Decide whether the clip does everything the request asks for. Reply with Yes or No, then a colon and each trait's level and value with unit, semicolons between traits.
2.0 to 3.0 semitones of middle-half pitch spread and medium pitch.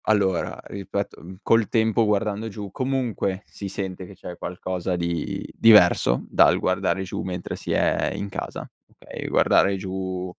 No: narrow, 2.4 semitones; very low, 95 Hz